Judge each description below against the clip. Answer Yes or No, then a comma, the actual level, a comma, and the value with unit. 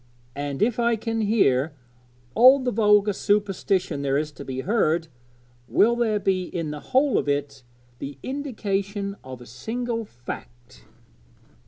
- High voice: Yes, high, 200 Hz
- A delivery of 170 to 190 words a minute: No, average, 145 wpm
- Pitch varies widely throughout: Yes, wide, 7.9 semitones